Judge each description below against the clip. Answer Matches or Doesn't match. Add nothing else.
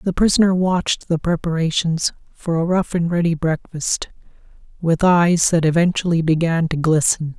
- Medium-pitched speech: Matches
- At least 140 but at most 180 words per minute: Matches